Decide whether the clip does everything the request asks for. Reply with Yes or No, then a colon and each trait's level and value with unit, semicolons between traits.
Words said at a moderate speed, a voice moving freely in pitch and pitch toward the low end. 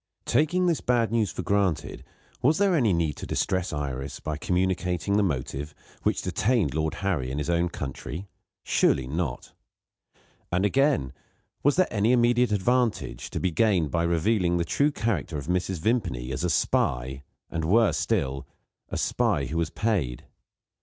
Yes: average, 160 wpm; wide, 6.9 semitones; very low, 90 Hz